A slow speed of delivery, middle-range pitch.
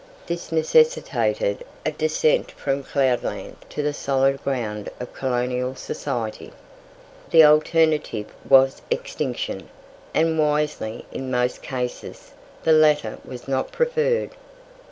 Yes: slow, 110 wpm; medium, 145 Hz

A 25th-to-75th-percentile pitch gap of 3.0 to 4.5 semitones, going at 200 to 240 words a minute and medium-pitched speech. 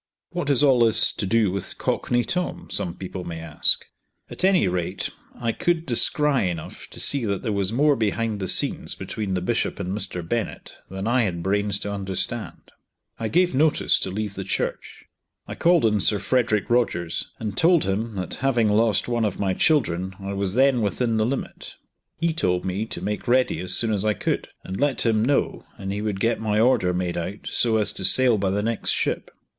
No: average, 4.2 semitones; fast, 205 wpm; low, 105 Hz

